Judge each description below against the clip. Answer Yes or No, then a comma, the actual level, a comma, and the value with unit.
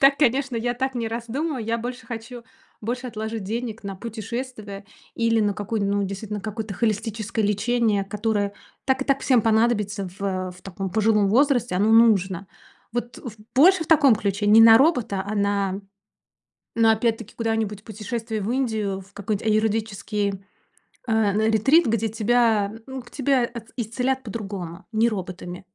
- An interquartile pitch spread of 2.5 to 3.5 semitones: Yes, average, 2.9 semitones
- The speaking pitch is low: No, high, 220 Hz